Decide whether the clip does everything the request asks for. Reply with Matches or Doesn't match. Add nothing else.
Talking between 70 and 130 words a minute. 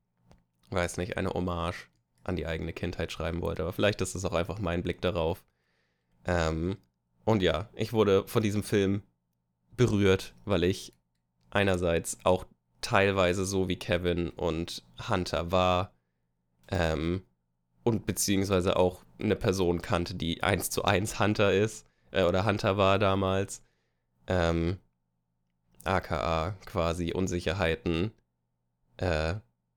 Matches